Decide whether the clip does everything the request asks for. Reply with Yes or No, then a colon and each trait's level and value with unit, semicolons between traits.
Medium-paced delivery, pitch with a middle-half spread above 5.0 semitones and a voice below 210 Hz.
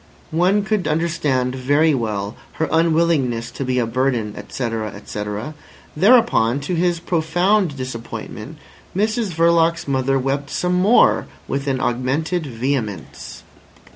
No: slow, 120 wpm; wide, 5.5 semitones; medium, 140 Hz